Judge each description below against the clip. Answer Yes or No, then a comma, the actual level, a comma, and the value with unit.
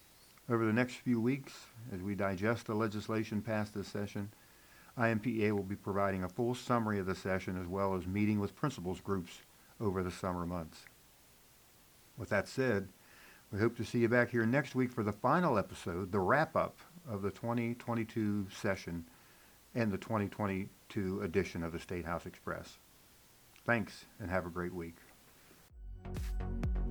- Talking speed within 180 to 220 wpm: No, average, 160 wpm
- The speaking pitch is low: Yes, low, 100 Hz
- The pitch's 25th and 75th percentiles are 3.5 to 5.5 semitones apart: Yes, average, 3.8 semitones